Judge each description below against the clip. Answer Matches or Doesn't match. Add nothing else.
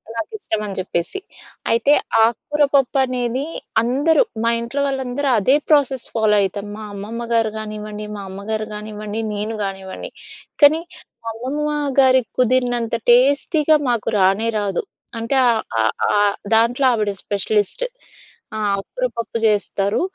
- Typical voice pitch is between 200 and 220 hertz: Doesn't match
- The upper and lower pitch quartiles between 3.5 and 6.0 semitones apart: Matches